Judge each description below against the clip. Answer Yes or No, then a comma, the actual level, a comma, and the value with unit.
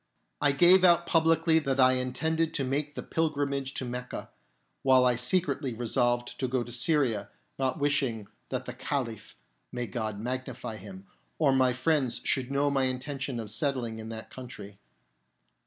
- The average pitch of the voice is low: Yes, low, 130 Hz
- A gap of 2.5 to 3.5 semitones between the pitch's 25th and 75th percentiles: Yes, average, 3.0 semitones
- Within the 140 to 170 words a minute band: Yes, average, 160 wpm